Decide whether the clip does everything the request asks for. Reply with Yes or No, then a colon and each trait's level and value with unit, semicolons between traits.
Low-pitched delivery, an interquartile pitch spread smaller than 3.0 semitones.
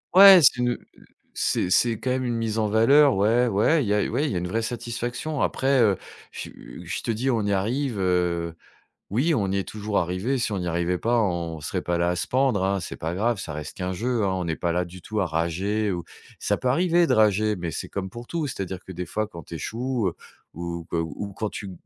No: low, 105 Hz; average, 5.2 semitones